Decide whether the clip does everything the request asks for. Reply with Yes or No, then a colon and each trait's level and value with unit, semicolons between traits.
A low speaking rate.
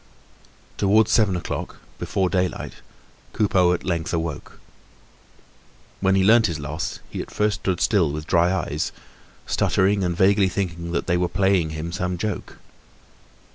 No: average, 145 wpm